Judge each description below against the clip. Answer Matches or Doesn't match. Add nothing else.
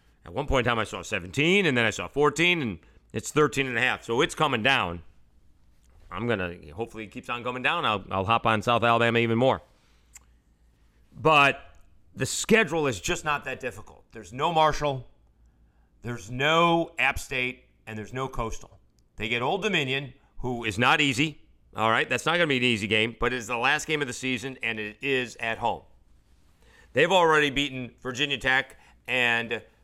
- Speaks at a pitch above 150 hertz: Doesn't match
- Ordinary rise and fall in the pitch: Doesn't match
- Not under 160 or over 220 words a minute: Matches